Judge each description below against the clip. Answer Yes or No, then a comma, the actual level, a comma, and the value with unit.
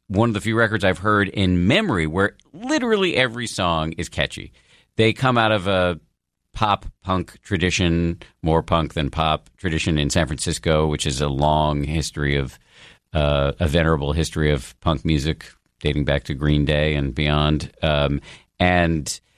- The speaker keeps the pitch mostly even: No, average, 4.2 semitones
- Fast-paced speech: No, average, 165 wpm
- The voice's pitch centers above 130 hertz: No, very low, 80 Hz